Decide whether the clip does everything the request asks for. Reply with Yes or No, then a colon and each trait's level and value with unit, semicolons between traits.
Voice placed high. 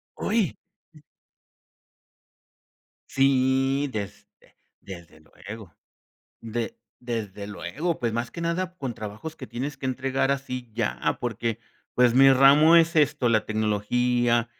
No: low, 125 Hz